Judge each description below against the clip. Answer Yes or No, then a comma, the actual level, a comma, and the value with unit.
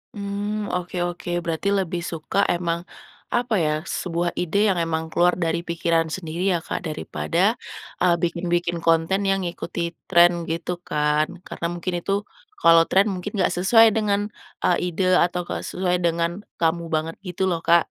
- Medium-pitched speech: Yes, medium, 175 Hz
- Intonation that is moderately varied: No, narrow, 2.1 semitones